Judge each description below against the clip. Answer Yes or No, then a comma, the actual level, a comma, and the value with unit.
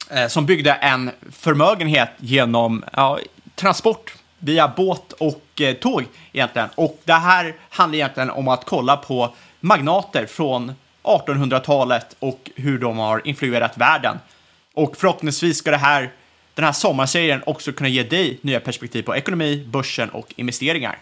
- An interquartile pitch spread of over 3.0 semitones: Yes, average, 3.7 semitones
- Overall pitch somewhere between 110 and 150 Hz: Yes, medium, 140 Hz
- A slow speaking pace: No, average, 140 wpm